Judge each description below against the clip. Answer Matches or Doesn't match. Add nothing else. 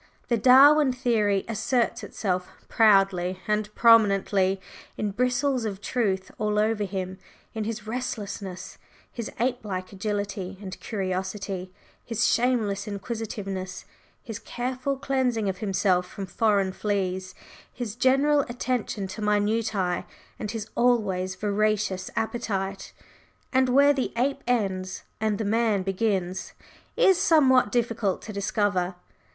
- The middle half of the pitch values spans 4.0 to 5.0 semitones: Doesn't match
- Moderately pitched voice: Doesn't match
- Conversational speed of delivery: Doesn't match